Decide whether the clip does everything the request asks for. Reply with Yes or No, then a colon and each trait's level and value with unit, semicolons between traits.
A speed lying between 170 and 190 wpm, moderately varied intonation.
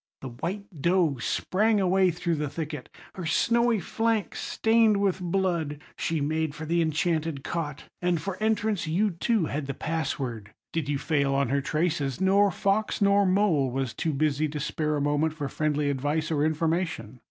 Yes: average, 175 wpm; average, 4.6 semitones